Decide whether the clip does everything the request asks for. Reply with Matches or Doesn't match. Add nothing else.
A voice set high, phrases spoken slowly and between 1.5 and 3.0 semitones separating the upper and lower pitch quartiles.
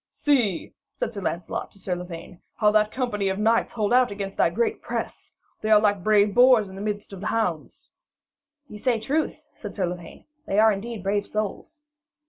Doesn't match